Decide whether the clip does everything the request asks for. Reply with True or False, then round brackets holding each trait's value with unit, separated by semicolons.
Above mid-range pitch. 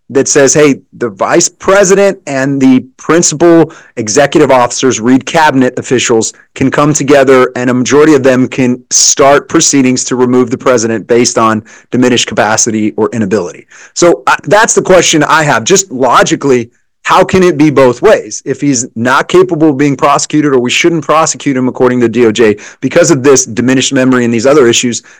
False (130 Hz)